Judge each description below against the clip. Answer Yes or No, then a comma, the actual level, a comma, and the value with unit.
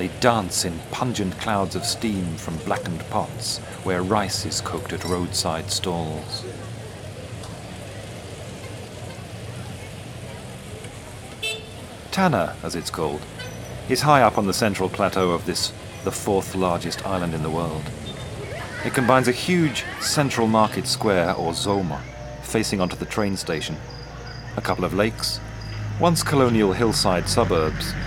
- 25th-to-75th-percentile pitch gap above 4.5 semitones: No, average, 3.9 semitones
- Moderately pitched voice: No, low, 105 Hz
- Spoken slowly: Yes, slow, 125 wpm